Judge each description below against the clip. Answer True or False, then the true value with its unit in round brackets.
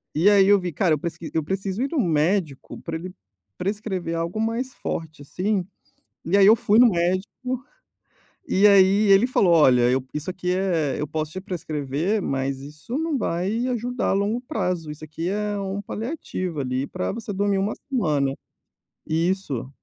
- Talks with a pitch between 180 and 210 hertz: True (185 Hz)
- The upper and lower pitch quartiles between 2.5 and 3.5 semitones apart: False (4.9 semitones)